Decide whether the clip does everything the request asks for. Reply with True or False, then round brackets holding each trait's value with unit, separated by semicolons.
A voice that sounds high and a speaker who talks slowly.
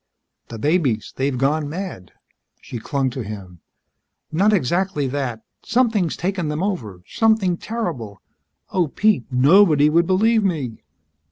False (155 Hz; 125 wpm)